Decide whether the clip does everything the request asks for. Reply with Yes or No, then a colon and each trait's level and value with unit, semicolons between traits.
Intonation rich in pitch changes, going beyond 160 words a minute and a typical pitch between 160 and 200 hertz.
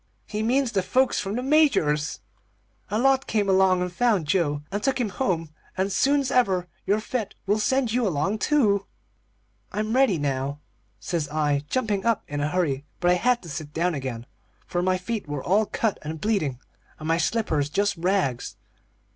Yes: wide, 6.4 semitones; average, 180 wpm; high, 190 Hz